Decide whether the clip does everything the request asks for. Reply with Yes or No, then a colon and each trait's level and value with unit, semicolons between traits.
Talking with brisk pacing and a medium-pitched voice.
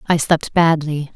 No: average, 155 wpm; medium, 155 Hz